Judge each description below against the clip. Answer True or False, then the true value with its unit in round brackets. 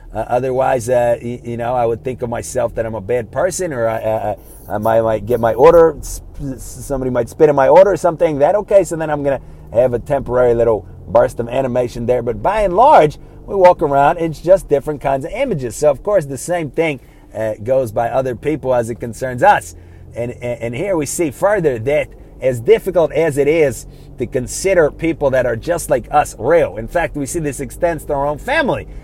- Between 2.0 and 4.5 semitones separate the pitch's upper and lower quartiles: False (5.5 semitones)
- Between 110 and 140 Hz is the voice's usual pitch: True (135 Hz)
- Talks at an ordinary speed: False (225 wpm)